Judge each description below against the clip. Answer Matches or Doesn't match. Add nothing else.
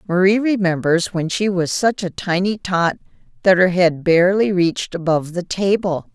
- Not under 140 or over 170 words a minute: Matches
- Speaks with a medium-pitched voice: Matches